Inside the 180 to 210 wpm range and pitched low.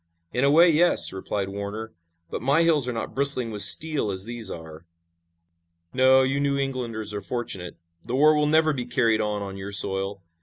Yes: average, 190 wpm; low, 120 Hz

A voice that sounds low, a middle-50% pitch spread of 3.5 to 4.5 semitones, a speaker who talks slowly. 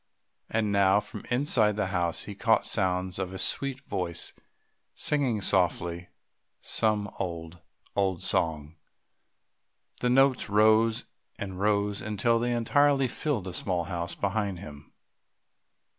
Yes: low, 100 Hz; average, 3.8 semitones; slow, 125 wpm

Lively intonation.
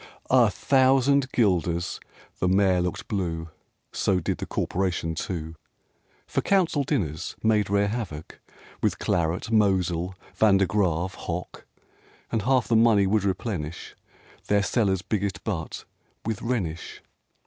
No: average, 4.1 semitones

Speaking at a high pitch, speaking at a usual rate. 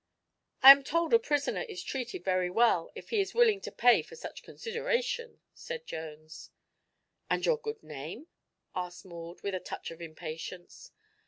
Yes: high, 240 Hz; average, 165 wpm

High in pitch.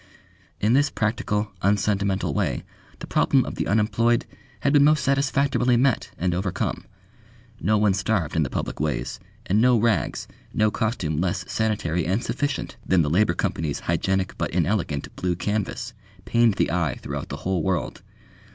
No: low, 105 Hz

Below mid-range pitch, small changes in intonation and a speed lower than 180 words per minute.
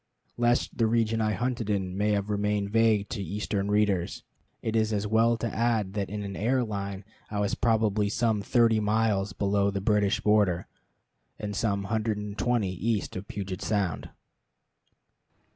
Yes: low, 105 Hz; narrow, 2.0 semitones; average, 165 wpm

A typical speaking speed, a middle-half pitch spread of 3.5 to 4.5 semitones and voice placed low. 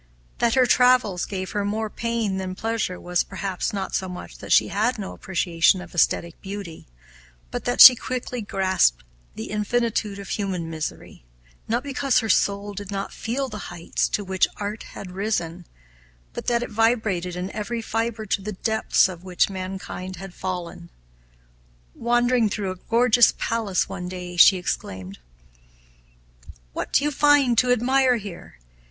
No: average, 160 wpm; average, 4.1 semitones; high, 200 Hz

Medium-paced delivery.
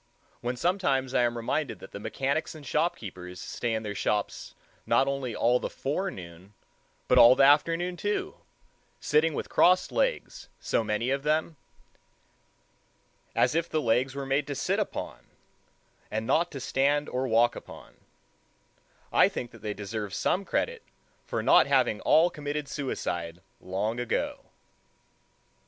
Yes: average, 145 wpm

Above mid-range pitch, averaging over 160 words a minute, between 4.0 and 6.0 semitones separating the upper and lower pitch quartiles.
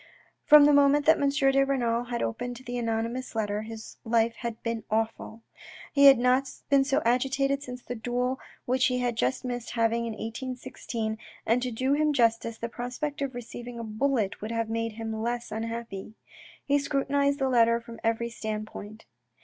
No: high, 240 Hz; average, 180 wpm; average, 2.9 semitones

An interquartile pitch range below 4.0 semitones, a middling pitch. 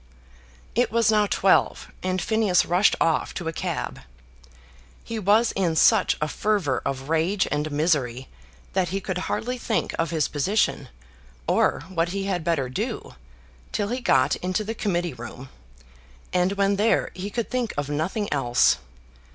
No: average, 5.3 semitones; medium, 180 Hz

